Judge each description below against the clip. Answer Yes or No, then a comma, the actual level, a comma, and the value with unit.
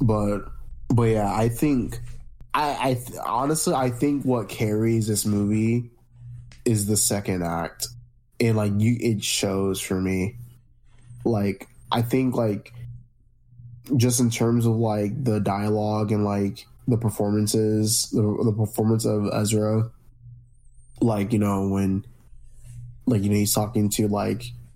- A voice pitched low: Yes, low, 115 Hz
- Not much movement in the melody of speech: Yes, narrow, 2.3 semitones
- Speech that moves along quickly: No, average, 140 wpm